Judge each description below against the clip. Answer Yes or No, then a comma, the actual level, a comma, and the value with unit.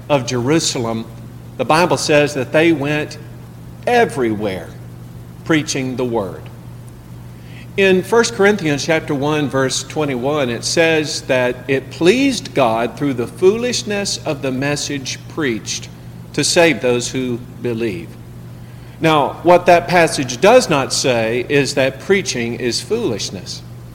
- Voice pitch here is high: No, low, 135 Hz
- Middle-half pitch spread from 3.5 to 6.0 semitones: Yes, average, 4.8 semitones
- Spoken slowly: Yes, slow, 125 wpm